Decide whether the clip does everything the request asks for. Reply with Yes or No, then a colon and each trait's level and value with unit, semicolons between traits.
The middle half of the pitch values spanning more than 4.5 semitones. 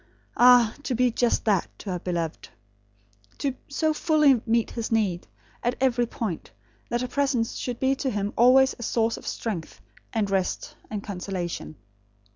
No: average, 3.9 semitones